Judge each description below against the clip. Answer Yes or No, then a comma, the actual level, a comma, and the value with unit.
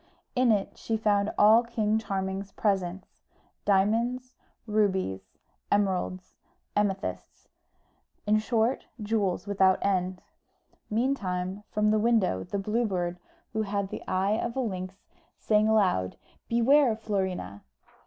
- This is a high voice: Yes, high, 205 Hz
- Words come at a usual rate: No, slow, 115 wpm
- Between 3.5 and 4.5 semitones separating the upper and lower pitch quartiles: No, average, 2.7 semitones